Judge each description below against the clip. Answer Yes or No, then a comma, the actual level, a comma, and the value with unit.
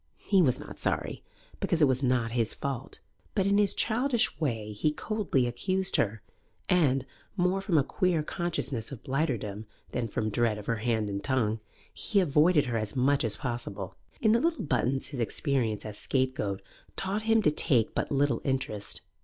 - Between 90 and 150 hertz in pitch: Yes, low, 135 Hz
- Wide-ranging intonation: Yes, wide, 7.5 semitones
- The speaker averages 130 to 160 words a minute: No, average, 180 wpm